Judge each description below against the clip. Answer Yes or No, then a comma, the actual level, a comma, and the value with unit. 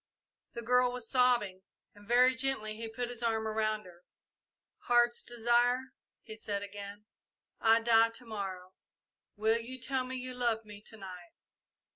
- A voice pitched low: No, high, 225 Hz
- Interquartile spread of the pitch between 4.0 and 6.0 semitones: No, narrow, 2.6 semitones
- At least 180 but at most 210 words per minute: No, average, 155 wpm